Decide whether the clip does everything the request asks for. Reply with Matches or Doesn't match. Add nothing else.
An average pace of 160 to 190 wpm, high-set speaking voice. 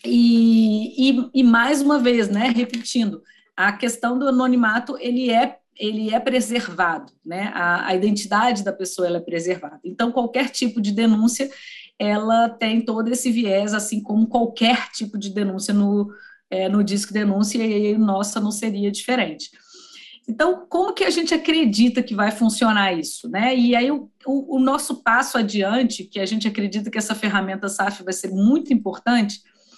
Matches